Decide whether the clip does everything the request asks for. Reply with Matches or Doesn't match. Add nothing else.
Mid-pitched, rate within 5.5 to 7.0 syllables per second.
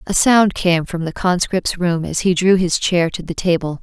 Doesn't match